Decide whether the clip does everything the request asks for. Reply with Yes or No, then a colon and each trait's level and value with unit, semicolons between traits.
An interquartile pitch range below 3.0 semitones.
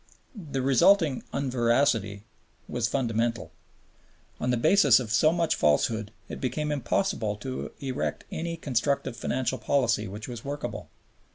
No: average, 3.9 semitones